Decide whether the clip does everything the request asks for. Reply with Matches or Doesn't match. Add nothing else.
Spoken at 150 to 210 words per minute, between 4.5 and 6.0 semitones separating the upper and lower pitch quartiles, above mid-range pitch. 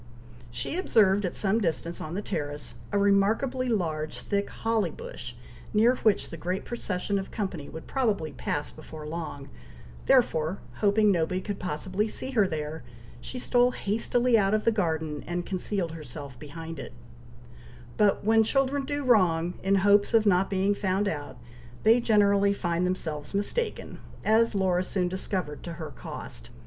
Matches